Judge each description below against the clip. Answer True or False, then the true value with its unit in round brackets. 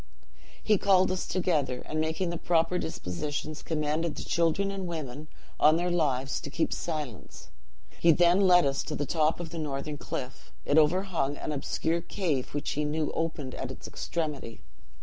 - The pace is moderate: True (170 wpm)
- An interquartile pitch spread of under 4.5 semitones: True (2.9 semitones)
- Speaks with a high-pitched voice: False (160 Hz)